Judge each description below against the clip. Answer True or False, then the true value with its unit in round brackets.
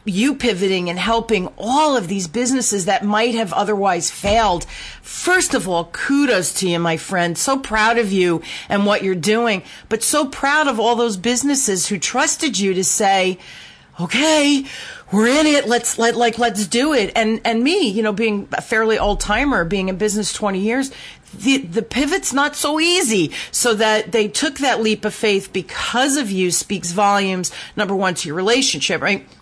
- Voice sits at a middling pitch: False (220 Hz)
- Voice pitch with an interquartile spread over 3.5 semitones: True (4.9 semitones)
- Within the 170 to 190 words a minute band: True (185 wpm)